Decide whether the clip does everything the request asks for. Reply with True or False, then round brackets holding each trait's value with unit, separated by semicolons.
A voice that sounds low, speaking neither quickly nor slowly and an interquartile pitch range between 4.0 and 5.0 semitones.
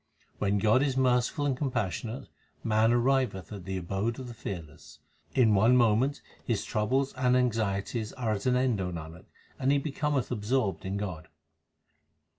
True (115 Hz; 160 wpm; 4.5 semitones)